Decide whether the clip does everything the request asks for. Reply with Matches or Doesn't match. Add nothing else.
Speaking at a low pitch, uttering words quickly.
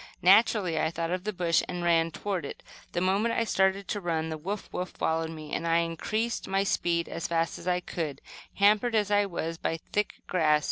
Doesn't match